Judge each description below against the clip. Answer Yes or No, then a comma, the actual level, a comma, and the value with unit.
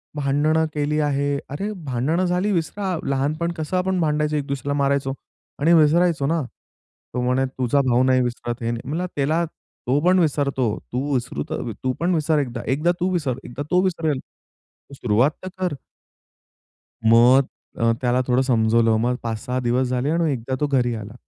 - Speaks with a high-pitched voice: No, medium, 140 Hz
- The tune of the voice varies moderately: Yes, average, 4.2 semitones